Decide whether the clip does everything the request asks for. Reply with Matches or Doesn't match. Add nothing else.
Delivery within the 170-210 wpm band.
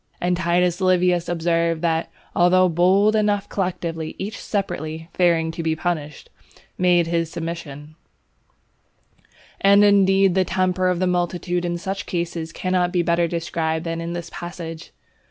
Doesn't match